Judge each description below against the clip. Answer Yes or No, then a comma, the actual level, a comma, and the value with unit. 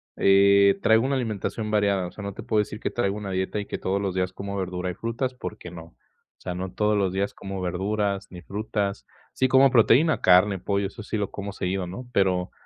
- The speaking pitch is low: Yes, low, 100 Hz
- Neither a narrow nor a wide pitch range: No, narrow, 2.2 semitones